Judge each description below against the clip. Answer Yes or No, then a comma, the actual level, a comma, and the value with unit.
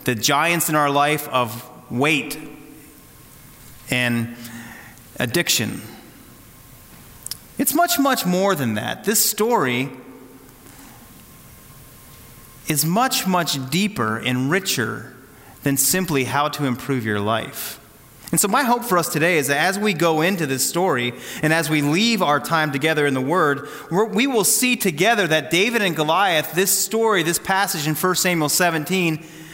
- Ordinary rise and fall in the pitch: No, wide, 5.8 semitones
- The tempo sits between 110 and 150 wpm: Yes, average, 145 wpm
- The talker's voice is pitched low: No, medium, 150 Hz